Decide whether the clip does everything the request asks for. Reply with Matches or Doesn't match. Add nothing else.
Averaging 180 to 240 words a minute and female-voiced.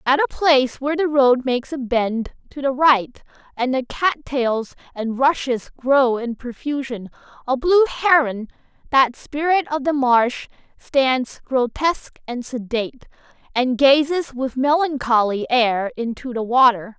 Doesn't match